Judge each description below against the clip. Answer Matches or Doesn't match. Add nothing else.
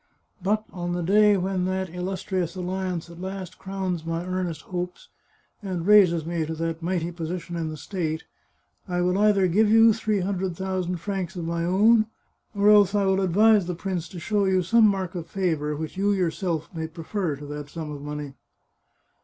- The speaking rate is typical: Matches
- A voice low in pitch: Doesn't match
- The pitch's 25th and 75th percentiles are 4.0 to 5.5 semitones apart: Doesn't match